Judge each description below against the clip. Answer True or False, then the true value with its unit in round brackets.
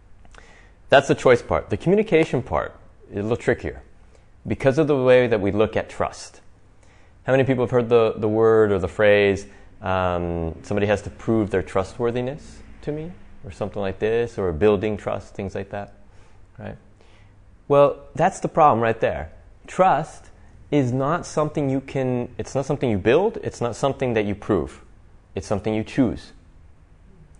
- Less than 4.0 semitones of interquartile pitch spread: False (4.7 semitones)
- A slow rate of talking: False (170 wpm)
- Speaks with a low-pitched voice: True (105 Hz)